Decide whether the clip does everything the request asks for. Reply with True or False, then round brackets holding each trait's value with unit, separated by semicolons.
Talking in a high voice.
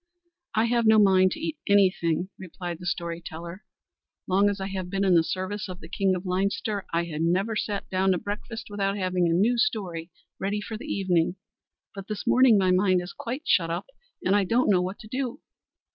True (195 Hz)